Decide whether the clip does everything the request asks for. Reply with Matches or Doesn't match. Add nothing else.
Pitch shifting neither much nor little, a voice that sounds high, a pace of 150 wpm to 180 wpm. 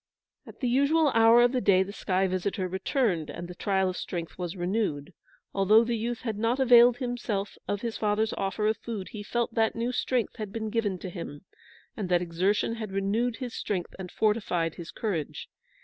Doesn't match